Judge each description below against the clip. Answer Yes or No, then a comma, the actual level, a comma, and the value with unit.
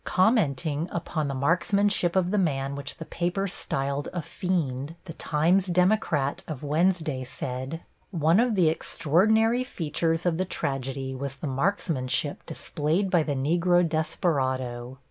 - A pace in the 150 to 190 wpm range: No, average, 140 wpm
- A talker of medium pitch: Yes, medium, 160 Hz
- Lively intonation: No, average, 4.6 semitones